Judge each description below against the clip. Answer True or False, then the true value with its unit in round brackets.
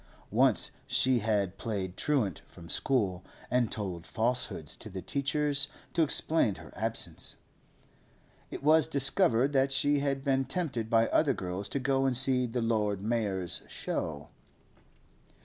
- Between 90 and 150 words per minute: True (140 wpm)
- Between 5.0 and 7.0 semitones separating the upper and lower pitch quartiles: True (5.3 semitones)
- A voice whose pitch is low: True (125 Hz)